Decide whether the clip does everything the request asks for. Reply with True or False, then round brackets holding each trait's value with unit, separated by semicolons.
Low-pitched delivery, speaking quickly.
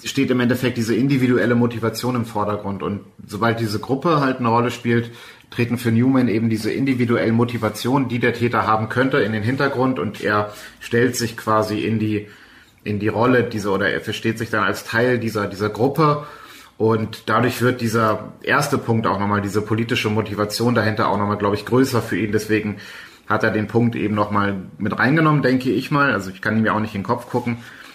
True (115 Hz; 200 wpm)